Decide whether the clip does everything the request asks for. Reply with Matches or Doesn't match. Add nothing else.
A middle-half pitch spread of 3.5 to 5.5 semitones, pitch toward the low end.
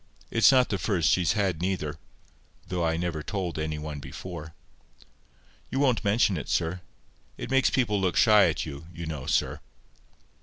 Matches